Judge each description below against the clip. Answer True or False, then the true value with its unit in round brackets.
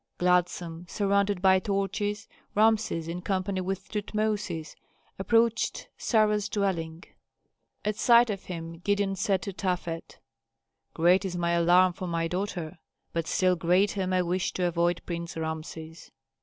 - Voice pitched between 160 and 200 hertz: True (185 Hz)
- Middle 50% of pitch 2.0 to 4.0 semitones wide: True (2.9 semitones)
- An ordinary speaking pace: False (130 wpm)